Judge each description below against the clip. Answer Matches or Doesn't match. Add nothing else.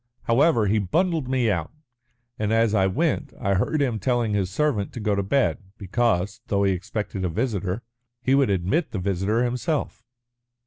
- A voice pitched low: Matches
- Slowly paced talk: Doesn't match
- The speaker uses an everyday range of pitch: Matches